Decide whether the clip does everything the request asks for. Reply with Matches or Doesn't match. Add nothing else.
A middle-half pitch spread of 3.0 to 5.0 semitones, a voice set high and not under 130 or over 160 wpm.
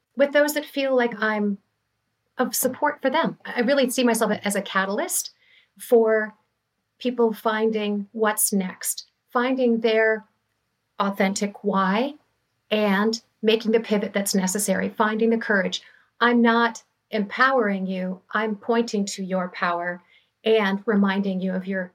Matches